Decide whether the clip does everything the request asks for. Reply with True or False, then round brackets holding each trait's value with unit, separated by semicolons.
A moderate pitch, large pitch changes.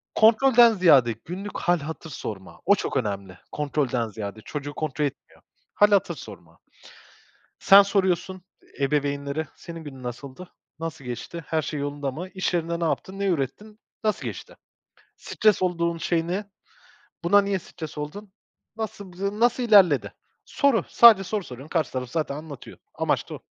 True (165 Hz; 5.8 semitones)